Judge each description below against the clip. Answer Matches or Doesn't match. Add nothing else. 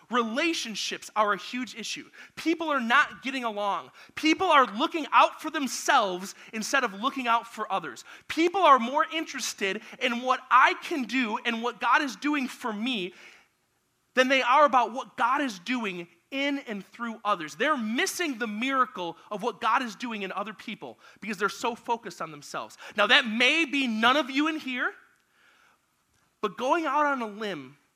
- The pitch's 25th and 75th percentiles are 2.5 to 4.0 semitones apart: Doesn't match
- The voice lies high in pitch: Matches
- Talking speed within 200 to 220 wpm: Doesn't match